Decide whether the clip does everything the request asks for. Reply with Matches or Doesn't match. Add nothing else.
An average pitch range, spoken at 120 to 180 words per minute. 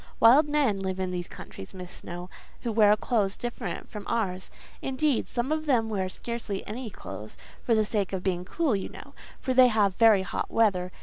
Doesn't match